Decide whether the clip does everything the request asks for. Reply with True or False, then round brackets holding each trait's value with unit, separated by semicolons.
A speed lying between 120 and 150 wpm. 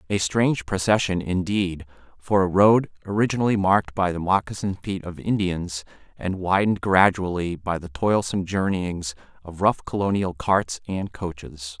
True (140 wpm)